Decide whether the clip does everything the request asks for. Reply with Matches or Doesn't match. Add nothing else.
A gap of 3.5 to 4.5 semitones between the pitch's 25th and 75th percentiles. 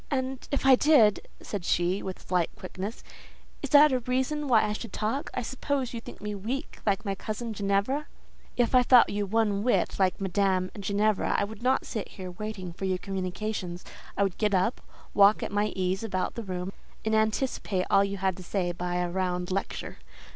Matches